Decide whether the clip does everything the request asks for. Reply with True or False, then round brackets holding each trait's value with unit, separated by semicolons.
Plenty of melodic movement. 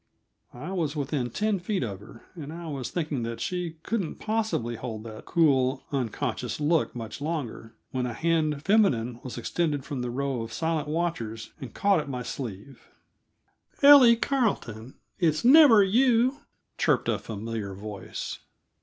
True (7.0 semitones)